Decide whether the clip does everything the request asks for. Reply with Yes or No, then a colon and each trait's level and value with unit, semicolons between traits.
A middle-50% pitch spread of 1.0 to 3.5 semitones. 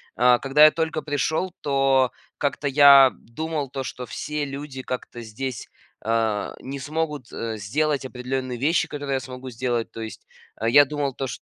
Yes: average, 2.8 semitones